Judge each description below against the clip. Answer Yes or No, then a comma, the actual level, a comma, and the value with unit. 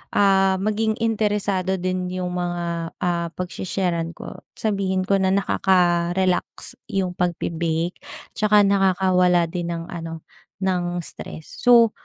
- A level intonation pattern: Yes, narrow, 2.1 semitones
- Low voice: No, medium, 185 Hz